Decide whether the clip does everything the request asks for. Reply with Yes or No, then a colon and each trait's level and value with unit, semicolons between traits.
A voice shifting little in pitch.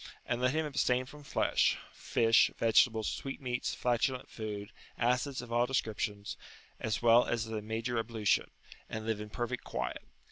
Yes: narrow, 2.3 semitones